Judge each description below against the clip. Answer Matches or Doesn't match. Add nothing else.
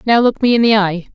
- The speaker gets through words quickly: Matches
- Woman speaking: Matches